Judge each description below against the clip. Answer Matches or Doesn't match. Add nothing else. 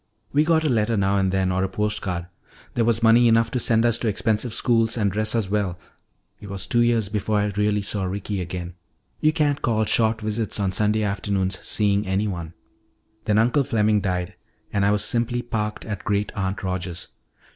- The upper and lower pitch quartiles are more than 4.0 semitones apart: Doesn't match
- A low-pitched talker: Matches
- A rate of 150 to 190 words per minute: Doesn't match